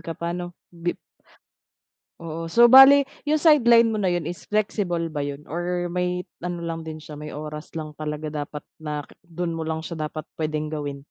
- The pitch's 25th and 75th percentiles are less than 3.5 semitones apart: Yes, average, 2.7 semitones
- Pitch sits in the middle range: Yes, medium, 165 Hz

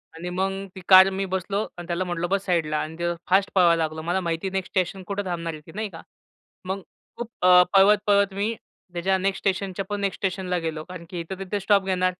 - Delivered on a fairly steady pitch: Yes, narrow, 2.2 semitones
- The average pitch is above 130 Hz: Yes, medium, 185 Hz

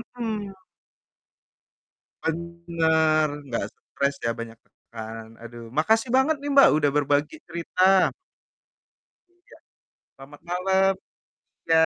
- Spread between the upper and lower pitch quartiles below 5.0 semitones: No, average, 5.3 semitones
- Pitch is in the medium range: Yes, medium, 165 Hz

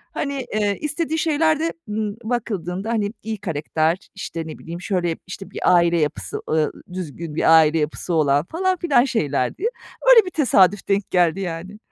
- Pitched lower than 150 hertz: No, high, 195 Hz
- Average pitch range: No, wide, 6.9 semitones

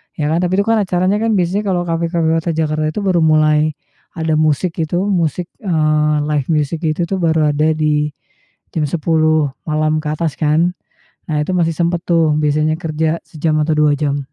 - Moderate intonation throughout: No, narrow, 2.0 semitones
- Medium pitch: Yes, medium, 155 Hz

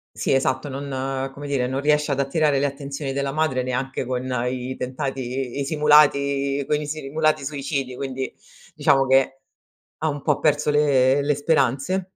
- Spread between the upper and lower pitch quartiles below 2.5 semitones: Yes, narrow, 1.9 semitones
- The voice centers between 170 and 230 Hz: No, medium, 140 Hz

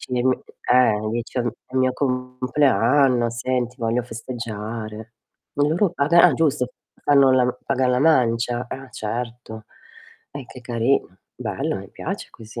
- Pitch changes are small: Yes, narrow, 2.1 semitones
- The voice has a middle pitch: No, low, 125 Hz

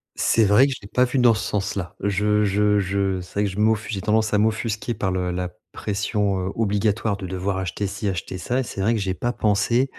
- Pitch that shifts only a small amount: Yes, narrow, 2.3 semitones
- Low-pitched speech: Yes, low, 105 Hz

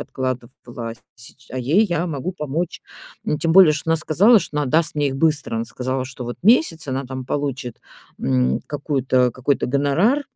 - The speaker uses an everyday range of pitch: Yes, average, 4.1 semitones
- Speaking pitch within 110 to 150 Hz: Yes, medium, 140 Hz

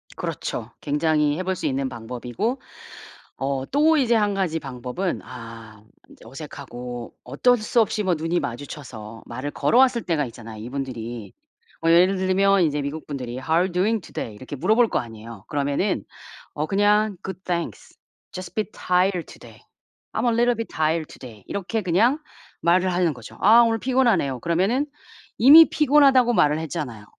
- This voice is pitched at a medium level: Yes, medium, 170 Hz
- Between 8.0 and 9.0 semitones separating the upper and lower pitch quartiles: Yes, wide, 8.5 semitones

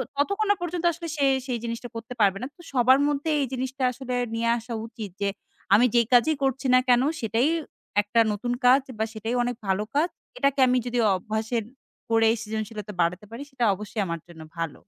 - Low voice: No, high, 240 Hz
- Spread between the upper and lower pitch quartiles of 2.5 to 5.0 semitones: Yes, average, 3.5 semitones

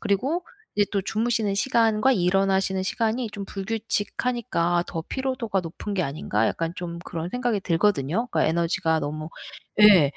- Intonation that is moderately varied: Yes, average, 4.9 semitones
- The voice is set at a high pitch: Yes, high, 195 Hz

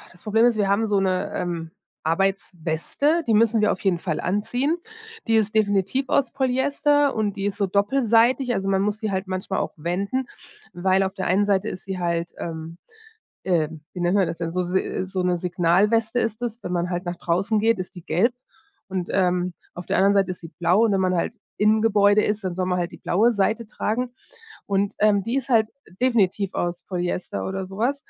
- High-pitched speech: Yes, high, 195 Hz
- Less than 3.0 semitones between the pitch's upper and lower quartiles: No, average, 3.6 semitones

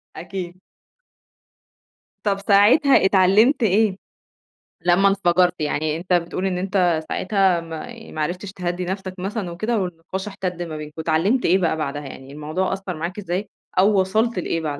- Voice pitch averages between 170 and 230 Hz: Yes, medium, 185 Hz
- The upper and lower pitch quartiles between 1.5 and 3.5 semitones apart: Yes, average, 2.8 semitones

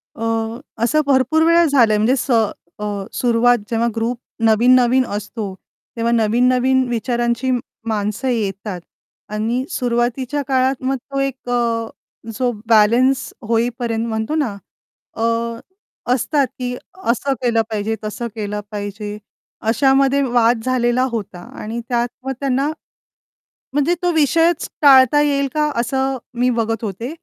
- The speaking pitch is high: Yes, high, 240 Hz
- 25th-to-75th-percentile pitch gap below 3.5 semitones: Yes, average, 2.9 semitones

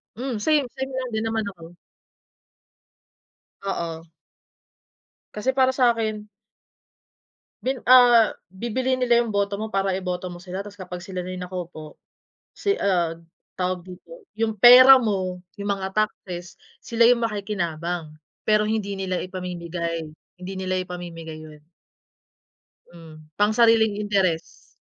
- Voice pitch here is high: Yes, high, 195 Hz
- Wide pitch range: No, average, 4.1 semitones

